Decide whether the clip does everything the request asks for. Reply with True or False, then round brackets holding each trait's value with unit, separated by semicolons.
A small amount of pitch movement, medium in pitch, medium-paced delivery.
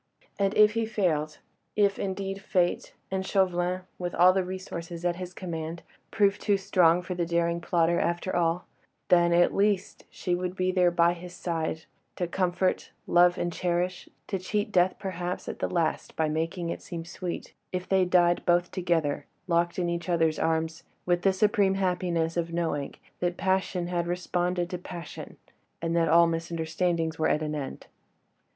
True (1.6 semitones; 175 Hz; 170 wpm)